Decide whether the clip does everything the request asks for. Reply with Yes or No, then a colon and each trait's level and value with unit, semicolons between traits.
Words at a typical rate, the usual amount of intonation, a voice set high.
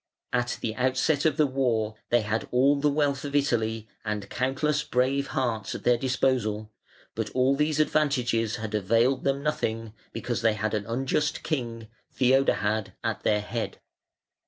No: average, 155 wpm; average, 3.8 semitones; low, 125 Hz